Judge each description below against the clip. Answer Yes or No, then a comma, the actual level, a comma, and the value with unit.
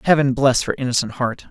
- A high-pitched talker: No, low, 130 Hz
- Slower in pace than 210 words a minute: Yes, average, 200 wpm